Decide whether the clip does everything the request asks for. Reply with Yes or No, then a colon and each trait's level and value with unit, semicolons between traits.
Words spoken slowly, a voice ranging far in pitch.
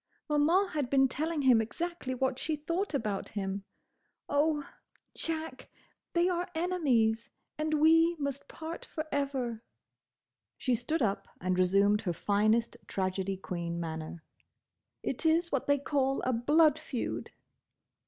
Yes: slow, 130 wpm; wide, 6.6 semitones